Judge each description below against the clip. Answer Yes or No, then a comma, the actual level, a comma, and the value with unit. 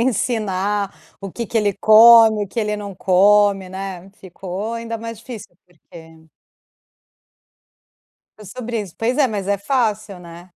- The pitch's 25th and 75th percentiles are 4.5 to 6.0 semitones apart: No, average, 3.1 semitones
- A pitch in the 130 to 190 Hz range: No, high, 205 Hz